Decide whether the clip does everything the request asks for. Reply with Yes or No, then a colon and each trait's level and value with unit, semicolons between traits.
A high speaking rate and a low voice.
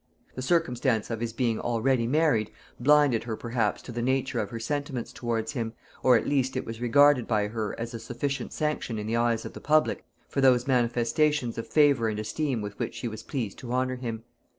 Yes: fast, 210 wpm; low, 120 Hz